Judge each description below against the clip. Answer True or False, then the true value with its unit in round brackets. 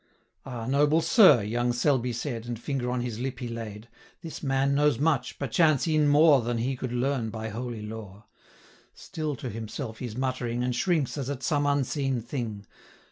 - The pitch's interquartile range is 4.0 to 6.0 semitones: False (3.5 semitones)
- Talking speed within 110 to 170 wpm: False (185 wpm)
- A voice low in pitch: True (125 Hz)